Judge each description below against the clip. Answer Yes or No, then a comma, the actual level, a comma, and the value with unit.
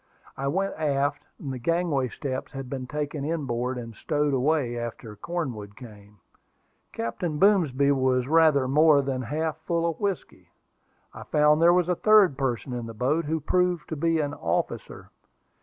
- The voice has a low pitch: No, medium, 145 Hz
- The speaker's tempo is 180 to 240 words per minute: No, average, 165 wpm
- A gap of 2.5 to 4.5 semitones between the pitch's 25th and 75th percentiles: Yes, average, 4.2 semitones